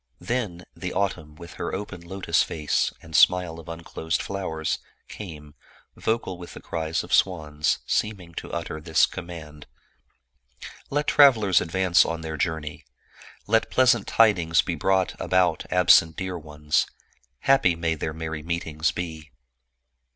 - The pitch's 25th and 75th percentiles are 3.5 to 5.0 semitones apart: No, average, 3.0 semitones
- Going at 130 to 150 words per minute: Yes, average, 145 wpm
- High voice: No, very low, 85 Hz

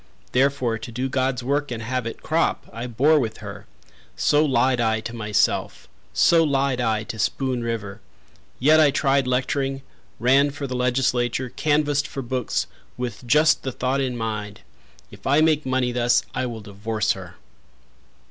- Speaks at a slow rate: No, average, 165 wpm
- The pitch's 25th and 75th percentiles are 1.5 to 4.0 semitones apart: Yes, average, 3.3 semitones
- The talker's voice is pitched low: Yes, low, 125 Hz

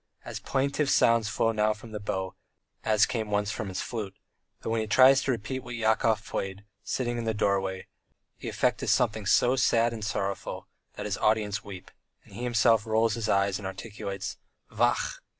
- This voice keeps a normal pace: Yes, average, 185 wpm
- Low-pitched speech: Yes, low, 110 Hz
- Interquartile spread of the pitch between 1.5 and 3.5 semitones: Yes, narrow, 2.4 semitones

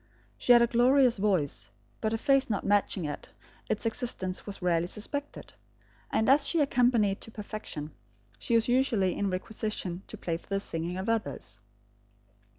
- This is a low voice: No, high, 215 Hz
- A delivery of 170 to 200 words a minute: No, average, 160 wpm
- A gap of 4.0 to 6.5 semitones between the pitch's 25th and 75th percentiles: Yes, average, 4.6 semitones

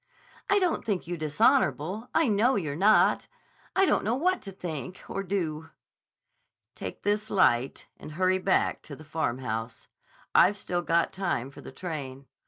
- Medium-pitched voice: Yes, medium, 180 Hz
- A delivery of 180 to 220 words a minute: No, average, 160 wpm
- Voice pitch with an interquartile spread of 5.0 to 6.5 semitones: Yes, wide, 5.4 semitones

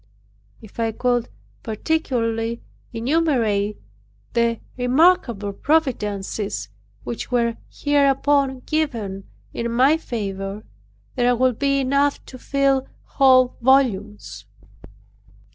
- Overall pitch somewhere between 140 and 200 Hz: No, high, 245 Hz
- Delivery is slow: Yes, slow, 90 wpm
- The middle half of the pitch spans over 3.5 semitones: Yes, average, 4.3 semitones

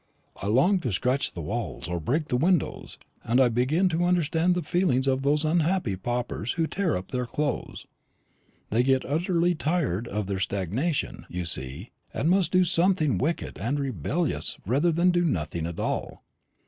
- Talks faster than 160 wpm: Yes, average, 175 wpm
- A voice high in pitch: No, medium, 140 Hz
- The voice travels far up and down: Yes, wide, 7.3 semitones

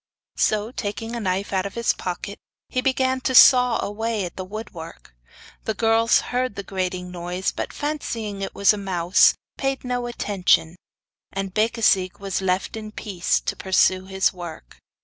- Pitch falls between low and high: No, high, 200 Hz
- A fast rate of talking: No, average, 160 wpm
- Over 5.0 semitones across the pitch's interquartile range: No, average, 3.7 semitones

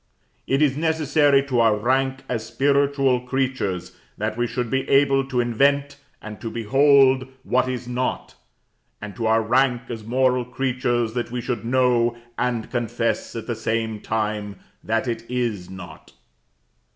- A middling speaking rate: Yes, average, 150 wpm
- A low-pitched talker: Yes, low, 125 Hz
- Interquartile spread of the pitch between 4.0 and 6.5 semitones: No, average, 2.8 semitones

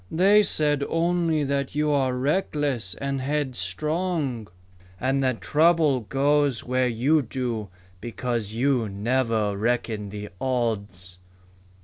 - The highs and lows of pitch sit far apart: No, average, 4.6 semitones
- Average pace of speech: No, slow, 110 wpm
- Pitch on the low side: Yes, low, 130 Hz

